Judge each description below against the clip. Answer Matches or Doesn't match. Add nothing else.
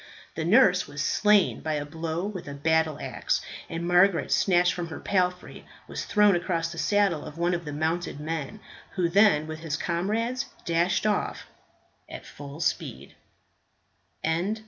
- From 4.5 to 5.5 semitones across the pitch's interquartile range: Doesn't match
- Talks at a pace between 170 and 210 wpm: Doesn't match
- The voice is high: Doesn't match